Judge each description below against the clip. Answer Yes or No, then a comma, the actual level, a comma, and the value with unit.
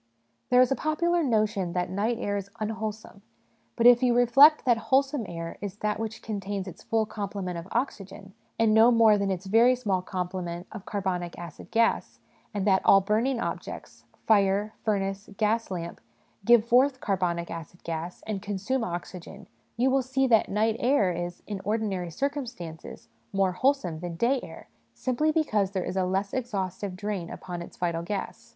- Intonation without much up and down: No, average, 4.2 semitones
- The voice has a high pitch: Yes, high, 205 Hz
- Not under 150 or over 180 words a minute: Yes, average, 170 wpm